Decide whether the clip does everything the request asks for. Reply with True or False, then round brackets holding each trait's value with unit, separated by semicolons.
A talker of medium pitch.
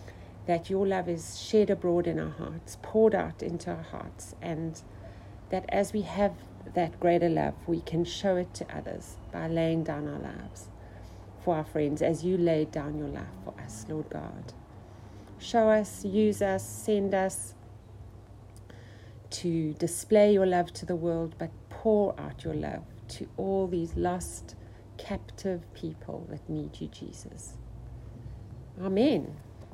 True (155 Hz)